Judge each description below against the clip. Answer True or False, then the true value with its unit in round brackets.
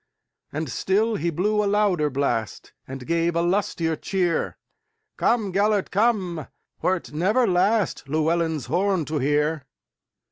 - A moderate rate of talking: False (110 wpm)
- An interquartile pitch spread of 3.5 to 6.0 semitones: True (4.8 semitones)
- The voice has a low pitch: False (175 Hz)